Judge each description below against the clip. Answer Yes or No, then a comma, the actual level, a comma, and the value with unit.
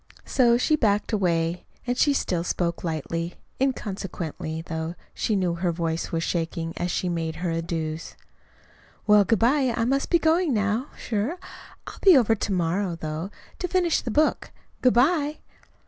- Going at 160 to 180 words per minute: Yes, average, 165 wpm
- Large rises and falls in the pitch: Yes, wide, 7.1 semitones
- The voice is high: Yes, high, 195 Hz